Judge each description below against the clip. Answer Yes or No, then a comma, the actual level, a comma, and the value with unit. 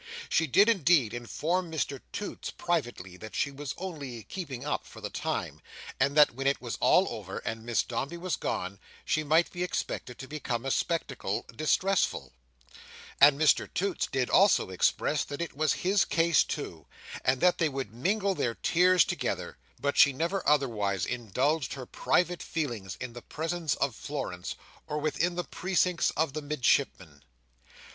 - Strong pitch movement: Yes, wide, 5.7 semitones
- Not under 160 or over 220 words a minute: Yes, average, 165 wpm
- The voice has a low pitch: No, medium, 145 Hz